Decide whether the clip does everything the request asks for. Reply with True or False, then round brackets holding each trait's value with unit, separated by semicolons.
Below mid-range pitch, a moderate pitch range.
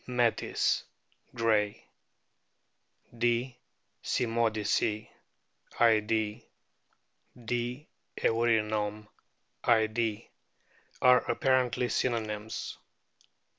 False (115 Hz; 2.0 semitones)